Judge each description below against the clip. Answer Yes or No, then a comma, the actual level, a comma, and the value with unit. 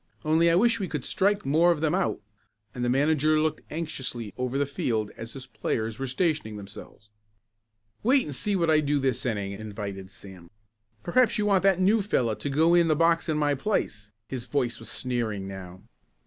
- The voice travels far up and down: Yes, wide, 7.1 semitones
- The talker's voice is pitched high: No, medium, 140 Hz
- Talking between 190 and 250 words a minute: Yes, average, 195 wpm